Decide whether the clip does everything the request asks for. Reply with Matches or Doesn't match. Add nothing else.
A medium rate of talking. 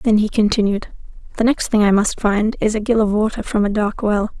Doesn't match